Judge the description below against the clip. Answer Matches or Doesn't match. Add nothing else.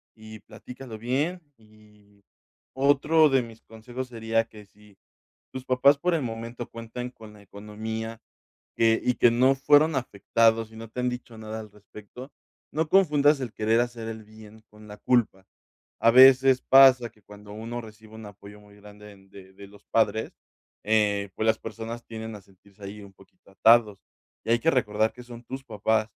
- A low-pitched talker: Matches